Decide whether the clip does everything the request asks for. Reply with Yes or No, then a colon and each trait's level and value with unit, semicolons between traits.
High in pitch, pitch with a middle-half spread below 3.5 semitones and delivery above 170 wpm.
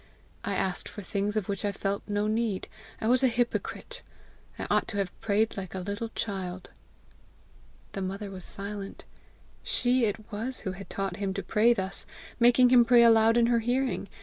Yes: high, 210 Hz; average, 3.1 semitones; average, 185 wpm